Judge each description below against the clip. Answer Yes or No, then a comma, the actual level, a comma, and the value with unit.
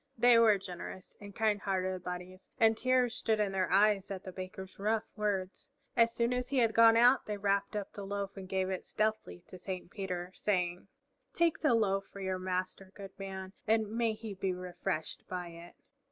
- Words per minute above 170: Yes, average, 195 wpm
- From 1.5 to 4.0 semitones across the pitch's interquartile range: Yes, average, 2.9 semitones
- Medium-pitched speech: No, high, 195 Hz